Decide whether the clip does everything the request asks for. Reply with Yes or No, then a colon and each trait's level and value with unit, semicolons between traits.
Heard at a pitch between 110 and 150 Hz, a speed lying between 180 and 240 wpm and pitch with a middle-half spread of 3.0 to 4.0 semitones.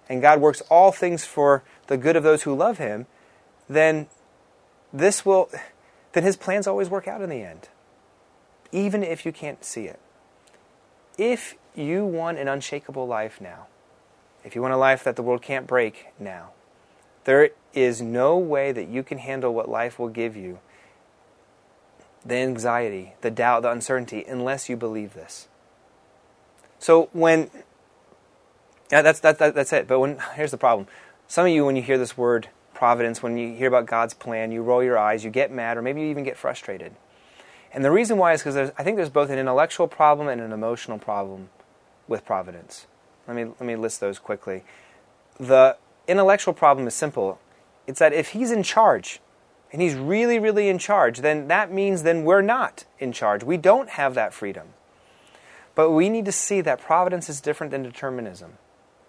No: medium, 140 Hz; average, 185 wpm; wide, 5.5 semitones